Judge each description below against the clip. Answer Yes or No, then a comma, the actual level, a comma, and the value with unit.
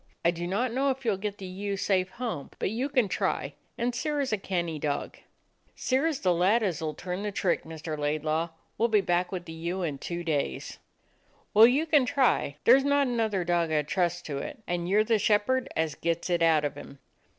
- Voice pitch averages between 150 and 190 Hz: Yes, medium, 185 Hz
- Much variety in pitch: Yes, wide, 5.9 semitones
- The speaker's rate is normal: No, fast, 230 wpm